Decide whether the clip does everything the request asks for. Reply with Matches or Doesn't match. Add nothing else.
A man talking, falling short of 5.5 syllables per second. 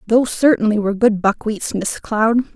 Doesn't match